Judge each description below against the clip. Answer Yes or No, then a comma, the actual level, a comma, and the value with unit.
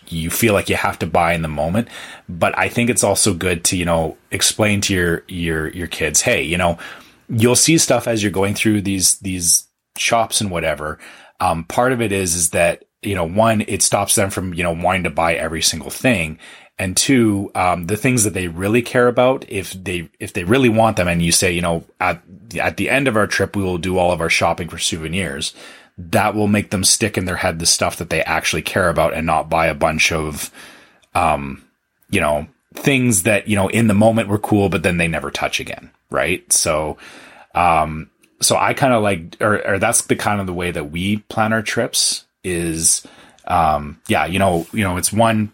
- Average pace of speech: No, fast, 225 wpm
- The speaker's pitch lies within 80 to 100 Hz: Yes, very low, 95 Hz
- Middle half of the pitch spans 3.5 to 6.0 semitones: Yes, average, 4.2 semitones